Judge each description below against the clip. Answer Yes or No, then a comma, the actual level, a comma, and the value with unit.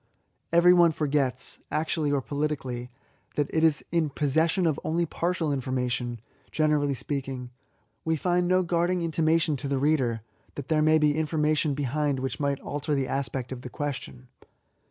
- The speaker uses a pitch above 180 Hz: No, medium, 150 Hz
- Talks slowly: No, average, 165 wpm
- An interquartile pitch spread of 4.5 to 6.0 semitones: No, average, 3.2 semitones